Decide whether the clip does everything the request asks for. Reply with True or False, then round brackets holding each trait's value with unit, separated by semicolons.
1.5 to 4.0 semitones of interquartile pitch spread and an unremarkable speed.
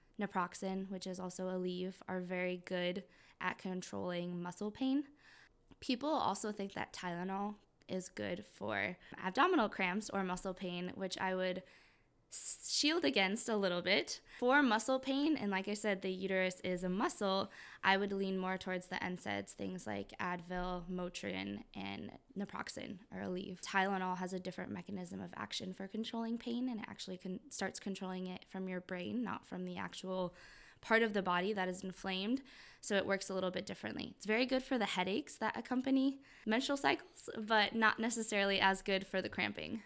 True (3.1 semitones; 175 wpm)